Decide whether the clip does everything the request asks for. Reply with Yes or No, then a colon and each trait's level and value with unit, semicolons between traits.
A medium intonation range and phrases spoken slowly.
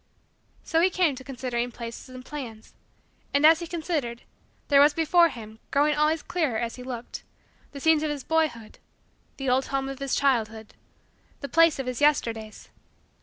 No: average, 4.4 semitones; average, 170 wpm